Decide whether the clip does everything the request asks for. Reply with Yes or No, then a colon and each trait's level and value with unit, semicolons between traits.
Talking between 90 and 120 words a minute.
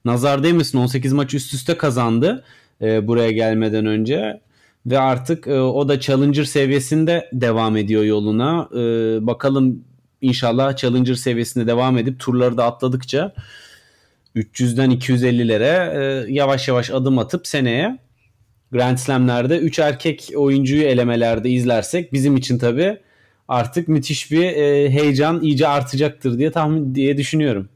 No: average, 130 wpm